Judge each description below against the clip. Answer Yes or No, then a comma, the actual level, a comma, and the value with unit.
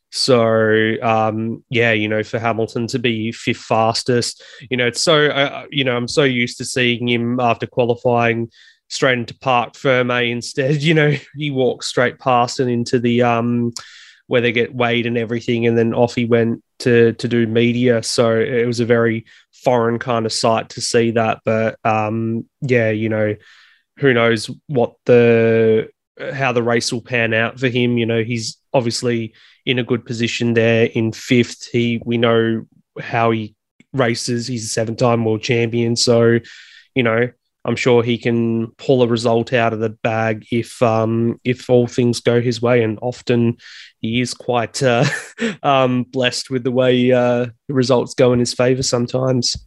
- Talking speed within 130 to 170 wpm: No, average, 180 wpm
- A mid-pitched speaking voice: No, low, 120 Hz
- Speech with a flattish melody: Yes, narrow, 1.4 semitones